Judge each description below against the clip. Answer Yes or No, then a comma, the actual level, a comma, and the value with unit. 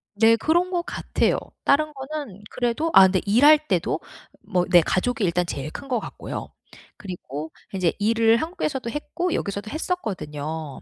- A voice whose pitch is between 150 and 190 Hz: No, high, 225 Hz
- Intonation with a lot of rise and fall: Yes, wide, 8.6 semitones